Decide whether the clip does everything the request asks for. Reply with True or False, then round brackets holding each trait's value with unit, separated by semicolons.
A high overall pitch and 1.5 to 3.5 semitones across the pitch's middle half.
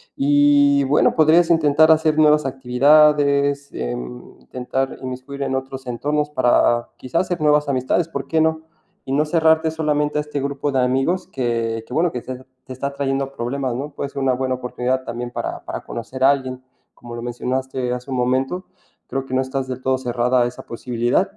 False (135 Hz; 2.7 semitones)